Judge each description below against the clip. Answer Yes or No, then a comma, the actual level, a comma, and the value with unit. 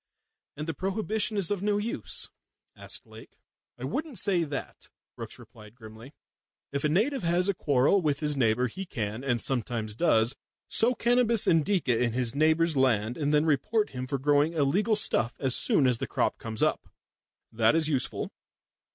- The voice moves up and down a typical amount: No, wide, 7.6 semitones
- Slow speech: No, average, 175 wpm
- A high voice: No, medium, 150 Hz